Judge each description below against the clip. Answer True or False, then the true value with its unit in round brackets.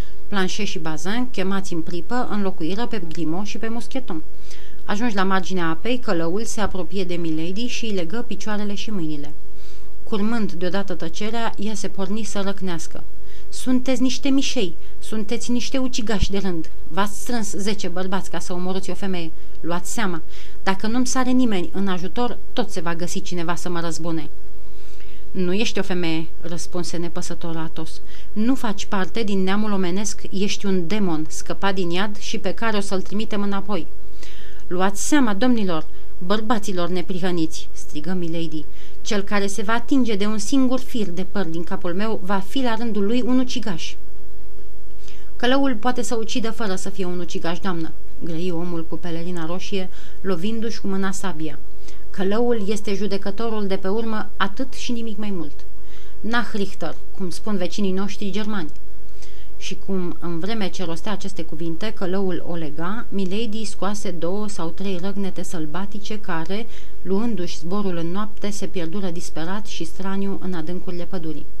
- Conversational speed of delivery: True (160 wpm)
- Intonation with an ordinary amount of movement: True (3.4 semitones)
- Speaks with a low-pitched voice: False (195 Hz)